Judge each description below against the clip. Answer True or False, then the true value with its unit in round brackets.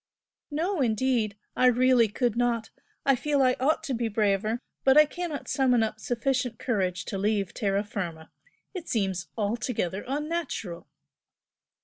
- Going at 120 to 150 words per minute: True (140 wpm)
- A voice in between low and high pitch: False (235 Hz)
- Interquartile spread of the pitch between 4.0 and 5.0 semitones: True (4.5 semitones)